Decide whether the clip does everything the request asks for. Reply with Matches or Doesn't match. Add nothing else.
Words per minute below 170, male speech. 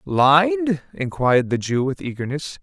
Matches